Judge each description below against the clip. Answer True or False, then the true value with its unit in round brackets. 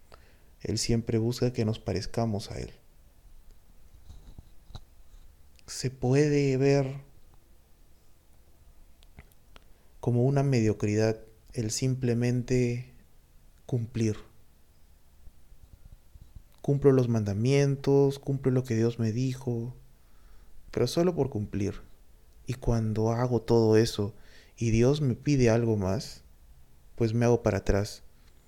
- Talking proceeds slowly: True (95 wpm)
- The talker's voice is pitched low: True (110 Hz)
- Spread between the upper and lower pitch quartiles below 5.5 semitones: False (8.2 semitones)